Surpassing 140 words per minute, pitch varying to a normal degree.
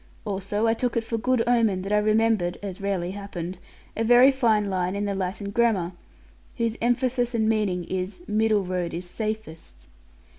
Yes: average, 175 wpm; average, 3.5 semitones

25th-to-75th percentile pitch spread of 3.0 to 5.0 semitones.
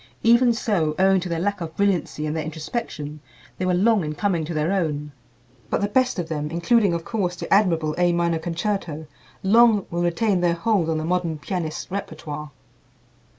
Yes: average, 4.0 semitones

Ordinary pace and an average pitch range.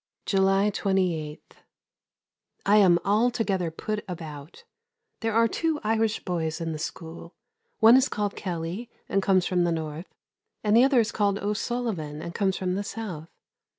Yes: average, 150 wpm; average, 4.5 semitones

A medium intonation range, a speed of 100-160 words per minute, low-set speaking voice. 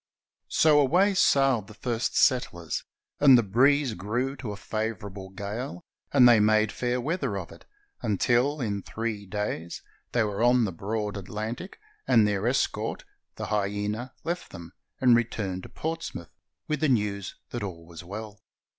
Yes: average, 4.0 semitones; average, 155 wpm; low, 110 Hz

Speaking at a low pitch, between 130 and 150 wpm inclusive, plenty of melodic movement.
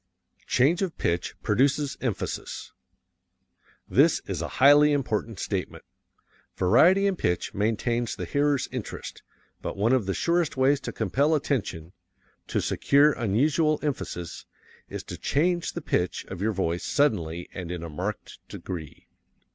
Yes: low, 120 Hz; average, 140 wpm; wide, 7.7 semitones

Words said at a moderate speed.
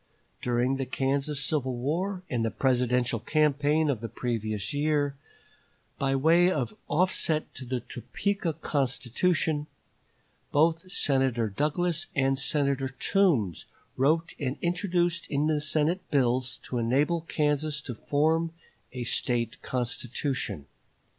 No: slow, 120 wpm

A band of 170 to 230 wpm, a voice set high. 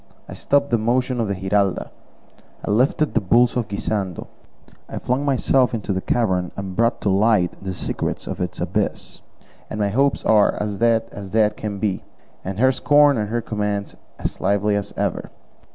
No: average, 185 wpm; low, 105 Hz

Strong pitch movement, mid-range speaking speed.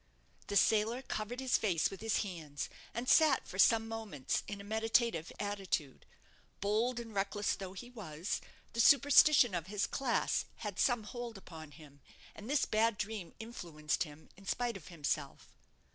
No: average, 4.8 semitones; average, 160 wpm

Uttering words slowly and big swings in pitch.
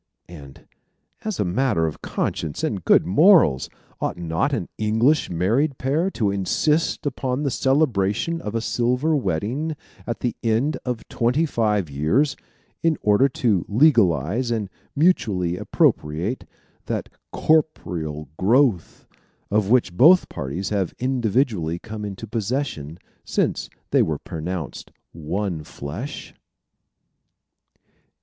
Yes: slow, 120 wpm; wide, 7.3 semitones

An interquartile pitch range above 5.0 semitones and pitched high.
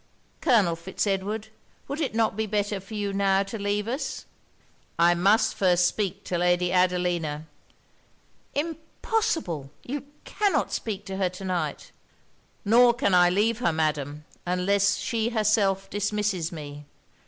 No: average, 3.7 semitones; high, 195 Hz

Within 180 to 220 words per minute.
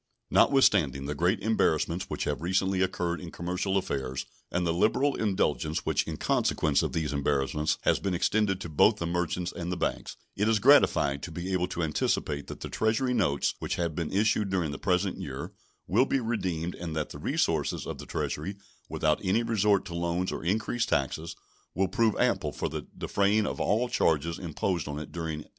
Yes: average, 190 wpm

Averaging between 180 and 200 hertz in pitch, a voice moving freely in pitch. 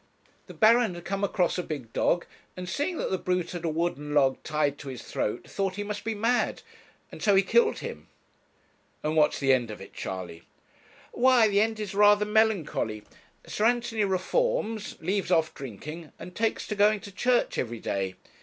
Yes: medium, 185 Hz; wide, 6.4 semitones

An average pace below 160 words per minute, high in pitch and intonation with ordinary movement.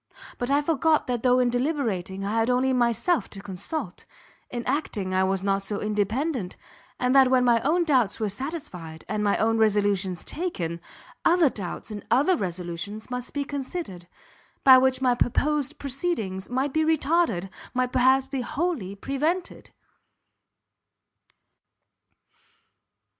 No: average, 140 wpm; high, 245 Hz; wide, 6.0 semitones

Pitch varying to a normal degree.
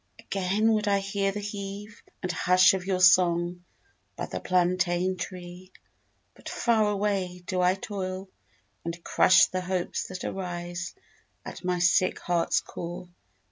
No: narrow, 1.7 semitones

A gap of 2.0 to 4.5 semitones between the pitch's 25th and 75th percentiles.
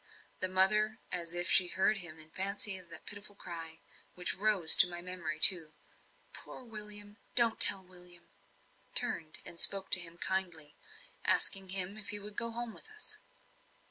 Yes: average, 3.1 semitones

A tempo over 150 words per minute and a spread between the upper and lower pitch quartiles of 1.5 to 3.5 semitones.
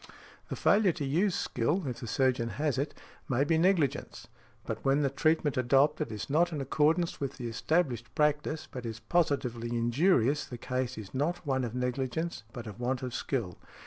No: average, 180 wpm; average, 4.3 semitones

